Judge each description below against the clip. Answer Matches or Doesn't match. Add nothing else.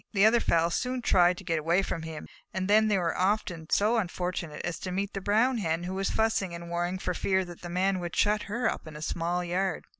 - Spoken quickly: Matches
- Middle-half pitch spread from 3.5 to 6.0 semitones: Doesn't match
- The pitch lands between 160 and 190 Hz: Matches